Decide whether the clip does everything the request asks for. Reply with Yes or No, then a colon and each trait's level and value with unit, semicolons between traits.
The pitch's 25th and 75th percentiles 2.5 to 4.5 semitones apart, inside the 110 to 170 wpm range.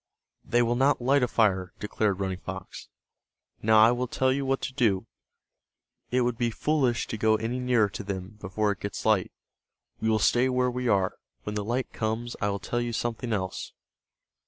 No: average, 3.2 semitones; average, 195 wpm